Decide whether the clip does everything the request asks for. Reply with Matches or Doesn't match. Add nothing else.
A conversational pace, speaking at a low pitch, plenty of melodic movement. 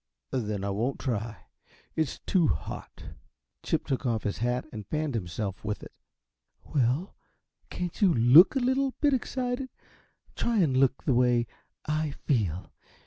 Matches